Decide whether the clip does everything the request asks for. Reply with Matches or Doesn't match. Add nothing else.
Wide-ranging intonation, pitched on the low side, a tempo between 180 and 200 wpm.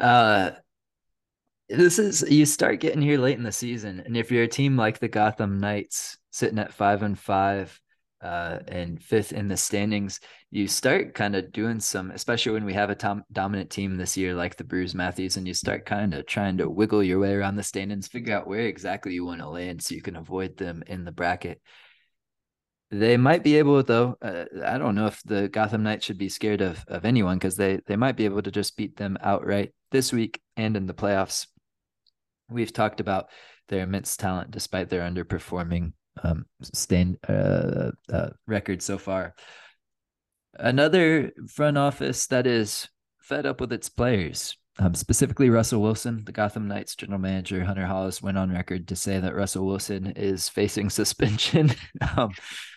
Doesn't match